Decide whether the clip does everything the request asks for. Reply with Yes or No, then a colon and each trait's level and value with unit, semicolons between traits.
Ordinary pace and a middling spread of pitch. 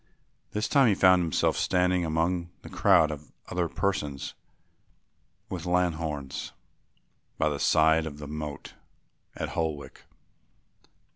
No: slow, 120 wpm; average, 3.1 semitones